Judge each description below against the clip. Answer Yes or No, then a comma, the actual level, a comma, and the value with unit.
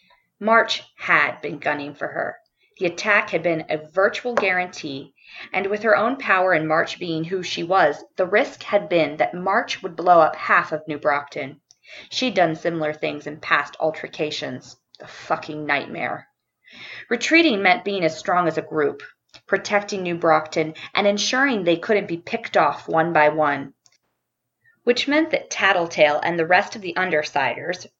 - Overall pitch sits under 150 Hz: No, medium, 175 Hz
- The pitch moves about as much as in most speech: Yes, average, 4.7 semitones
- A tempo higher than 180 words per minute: No, average, 165 wpm